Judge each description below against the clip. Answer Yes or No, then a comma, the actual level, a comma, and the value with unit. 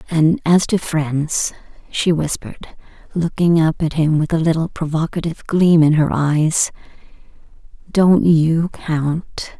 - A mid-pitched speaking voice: Yes, medium, 160 Hz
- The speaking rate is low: Yes, slow, 130 wpm